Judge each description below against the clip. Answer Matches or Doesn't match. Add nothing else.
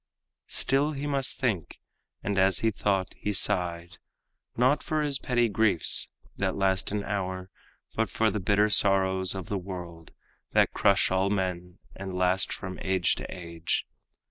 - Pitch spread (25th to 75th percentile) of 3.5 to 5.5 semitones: Doesn't match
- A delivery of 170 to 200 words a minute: Doesn't match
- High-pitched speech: Doesn't match